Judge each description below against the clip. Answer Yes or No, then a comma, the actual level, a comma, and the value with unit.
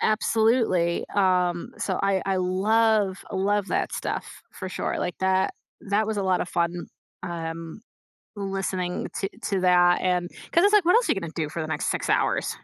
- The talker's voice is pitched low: No, high, 190 Hz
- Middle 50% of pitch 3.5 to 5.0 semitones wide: No, narrow, 2.6 semitones